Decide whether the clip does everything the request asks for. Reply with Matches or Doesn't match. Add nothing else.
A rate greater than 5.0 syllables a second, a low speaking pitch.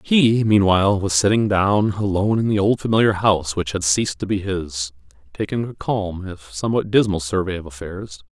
Matches